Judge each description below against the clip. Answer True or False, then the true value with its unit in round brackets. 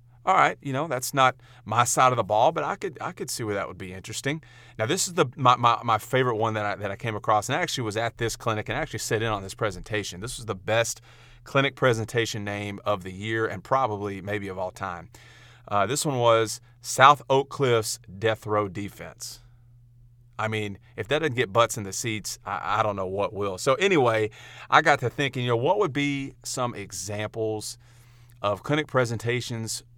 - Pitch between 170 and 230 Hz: False (115 Hz)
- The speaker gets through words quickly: True (220 wpm)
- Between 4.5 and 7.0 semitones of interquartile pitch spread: False (2.9 semitones)